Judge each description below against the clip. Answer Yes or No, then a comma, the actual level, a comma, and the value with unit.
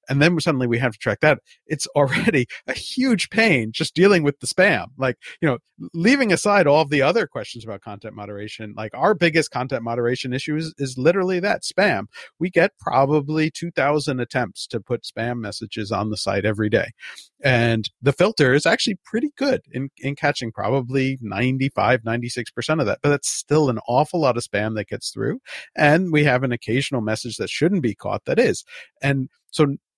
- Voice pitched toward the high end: No, low, 135 Hz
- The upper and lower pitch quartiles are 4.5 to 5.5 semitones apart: Yes, average, 5.1 semitones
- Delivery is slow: No, average, 190 wpm